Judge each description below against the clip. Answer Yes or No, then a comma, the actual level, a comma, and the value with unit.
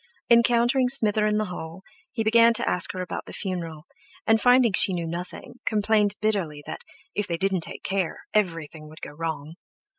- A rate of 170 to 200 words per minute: Yes, average, 185 wpm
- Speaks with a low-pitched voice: No, high, 195 Hz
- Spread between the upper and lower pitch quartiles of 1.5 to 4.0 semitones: No, average, 5.0 semitones